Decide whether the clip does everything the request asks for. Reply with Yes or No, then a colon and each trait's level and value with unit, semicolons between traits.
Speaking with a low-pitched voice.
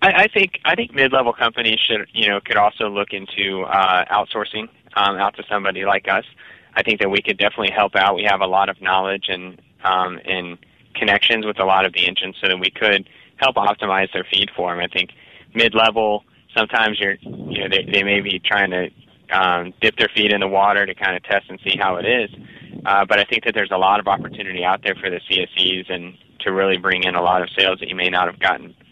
Yes: low, 100 Hz